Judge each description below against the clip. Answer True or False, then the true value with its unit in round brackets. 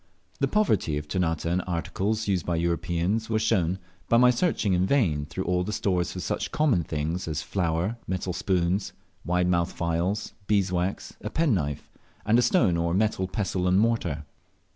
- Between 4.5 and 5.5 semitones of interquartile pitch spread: False (3.9 semitones)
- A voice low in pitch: True (90 Hz)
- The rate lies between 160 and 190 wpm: True (170 wpm)